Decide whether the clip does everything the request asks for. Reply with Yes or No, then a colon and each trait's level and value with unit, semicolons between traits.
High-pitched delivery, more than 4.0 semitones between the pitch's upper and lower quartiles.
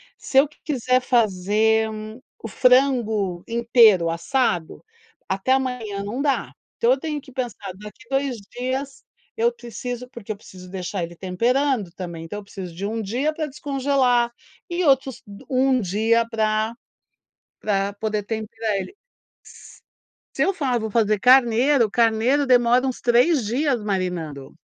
Yes: high, 230 Hz; average, 4.4 semitones